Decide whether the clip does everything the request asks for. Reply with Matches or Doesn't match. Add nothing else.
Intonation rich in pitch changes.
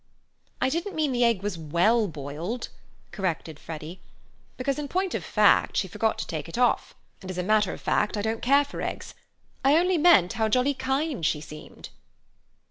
Matches